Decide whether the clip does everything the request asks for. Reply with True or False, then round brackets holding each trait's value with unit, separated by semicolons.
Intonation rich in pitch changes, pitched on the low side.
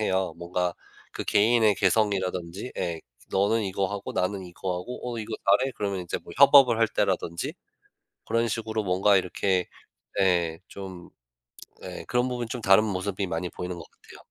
False (3.4 semitones; 95 Hz)